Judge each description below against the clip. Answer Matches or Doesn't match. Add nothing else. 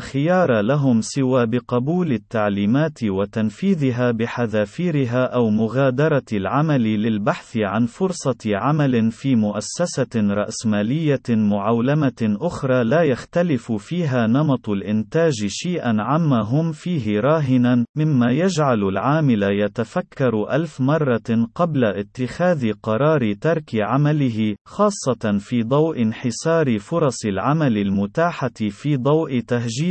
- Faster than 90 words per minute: Matches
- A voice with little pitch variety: Doesn't match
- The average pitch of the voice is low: Matches